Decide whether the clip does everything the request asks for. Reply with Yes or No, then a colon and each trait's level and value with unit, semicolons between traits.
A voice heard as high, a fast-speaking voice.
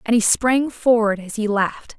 Yes: high, 225 Hz; fast, 210 wpm